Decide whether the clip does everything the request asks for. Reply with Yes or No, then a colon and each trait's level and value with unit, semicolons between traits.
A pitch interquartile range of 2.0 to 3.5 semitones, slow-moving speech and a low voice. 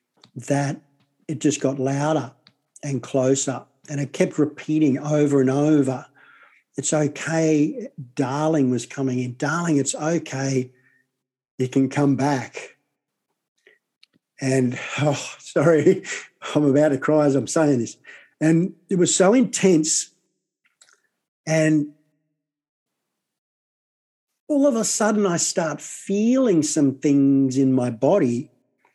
No: average, 2.7 semitones; slow, 120 wpm; medium, 145 Hz